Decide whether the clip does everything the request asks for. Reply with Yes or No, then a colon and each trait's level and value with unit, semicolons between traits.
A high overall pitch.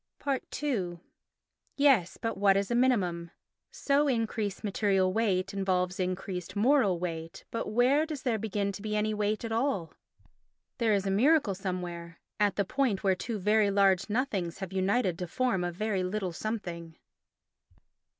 Yes: high, 200 Hz